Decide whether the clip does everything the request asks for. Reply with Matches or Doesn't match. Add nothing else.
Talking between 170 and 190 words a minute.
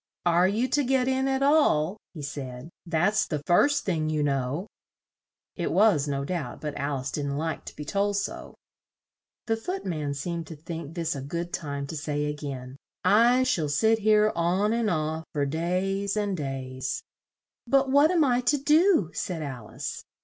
Matches